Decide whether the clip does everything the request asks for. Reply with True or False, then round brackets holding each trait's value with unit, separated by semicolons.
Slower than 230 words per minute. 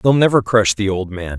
False (260 wpm)